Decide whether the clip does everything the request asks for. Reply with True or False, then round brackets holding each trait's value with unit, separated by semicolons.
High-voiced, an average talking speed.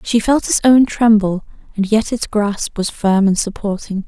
True (210 Hz; 190 wpm)